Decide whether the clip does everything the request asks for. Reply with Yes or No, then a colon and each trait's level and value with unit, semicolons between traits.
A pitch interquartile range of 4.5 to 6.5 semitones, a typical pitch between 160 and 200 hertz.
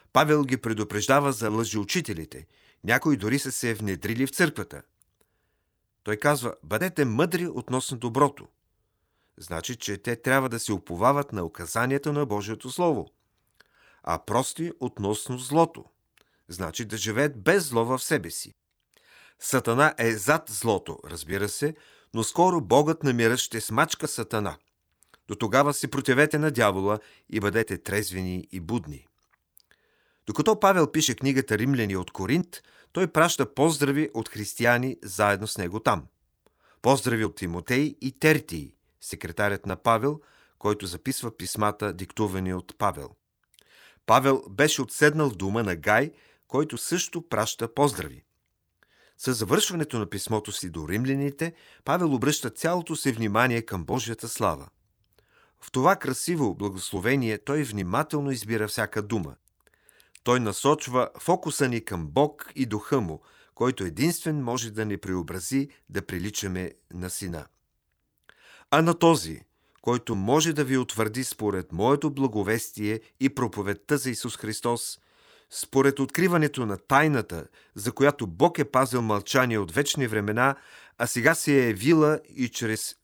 No: wide, 5.4 semitones; low, 120 Hz